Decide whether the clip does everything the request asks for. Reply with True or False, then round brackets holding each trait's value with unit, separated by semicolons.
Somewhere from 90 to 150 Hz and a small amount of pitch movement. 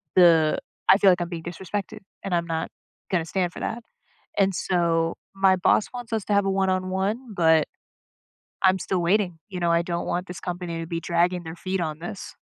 False (180 Hz; 2.3 semitones)